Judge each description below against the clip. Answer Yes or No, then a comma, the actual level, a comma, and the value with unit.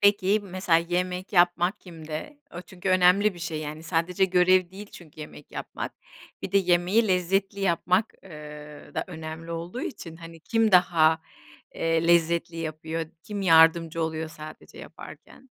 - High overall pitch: No, medium, 175 Hz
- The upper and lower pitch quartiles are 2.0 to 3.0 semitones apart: Yes, narrow, 2.5 semitones